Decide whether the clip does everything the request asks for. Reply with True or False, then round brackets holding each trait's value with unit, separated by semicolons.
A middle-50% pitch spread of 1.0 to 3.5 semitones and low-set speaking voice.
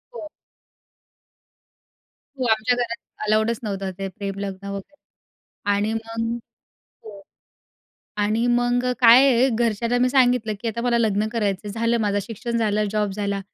False (2.8 semitones; 225 Hz)